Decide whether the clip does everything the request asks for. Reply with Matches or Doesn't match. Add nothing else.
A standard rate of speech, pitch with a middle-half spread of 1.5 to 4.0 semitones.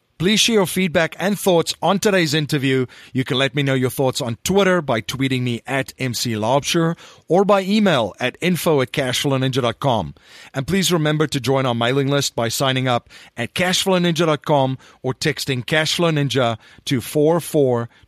Doesn't match